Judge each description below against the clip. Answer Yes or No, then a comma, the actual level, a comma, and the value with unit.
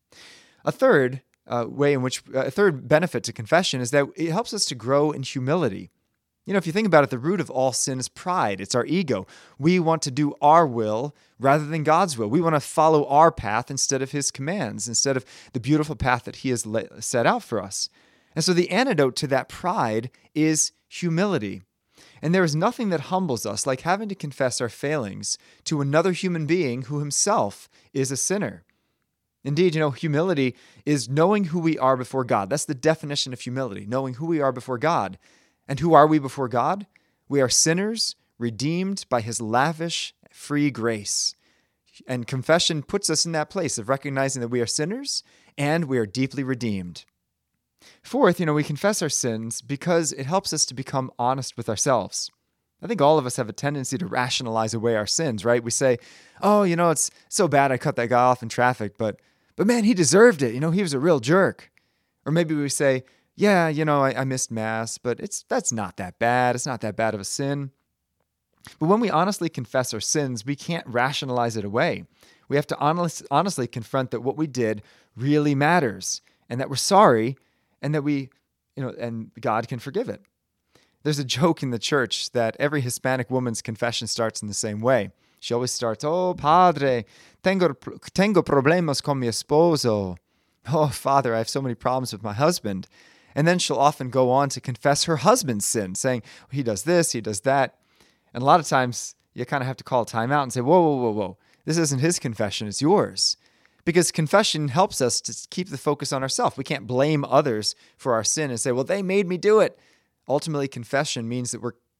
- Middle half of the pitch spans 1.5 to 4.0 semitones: No, average, 4.8 semitones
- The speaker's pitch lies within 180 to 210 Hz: No, low, 135 Hz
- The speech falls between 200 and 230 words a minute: Yes, fast, 205 wpm